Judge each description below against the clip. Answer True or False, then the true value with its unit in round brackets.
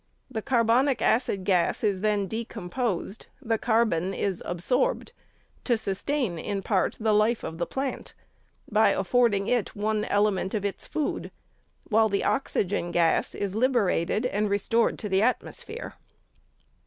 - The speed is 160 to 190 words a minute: False (140 wpm)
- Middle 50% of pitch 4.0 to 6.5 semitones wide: False (3.3 semitones)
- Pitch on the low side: False (215 Hz)